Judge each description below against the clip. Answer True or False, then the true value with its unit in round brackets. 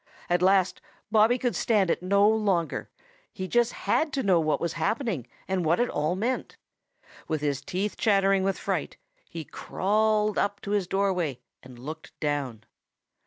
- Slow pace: False (165 wpm)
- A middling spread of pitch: True (4.6 semitones)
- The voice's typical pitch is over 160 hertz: True (190 Hz)